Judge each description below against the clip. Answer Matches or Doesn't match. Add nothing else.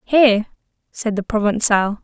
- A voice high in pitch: Matches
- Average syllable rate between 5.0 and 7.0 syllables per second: Doesn't match